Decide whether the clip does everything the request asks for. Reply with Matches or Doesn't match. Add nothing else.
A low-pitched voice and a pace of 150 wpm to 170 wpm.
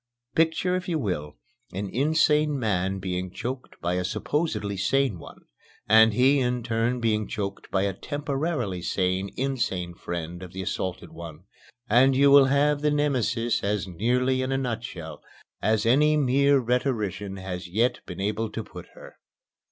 Matches